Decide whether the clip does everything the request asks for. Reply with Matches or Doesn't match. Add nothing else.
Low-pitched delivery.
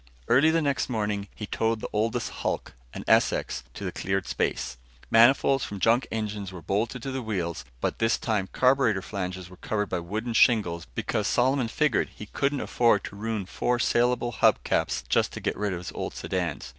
Matches